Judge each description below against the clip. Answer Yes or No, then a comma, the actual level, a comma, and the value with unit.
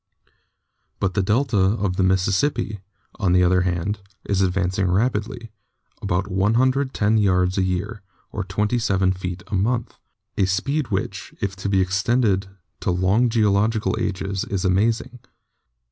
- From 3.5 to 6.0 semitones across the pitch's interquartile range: No, average, 3.1 semitones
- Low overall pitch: Yes, low, 100 Hz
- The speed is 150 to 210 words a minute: No, slow, 135 wpm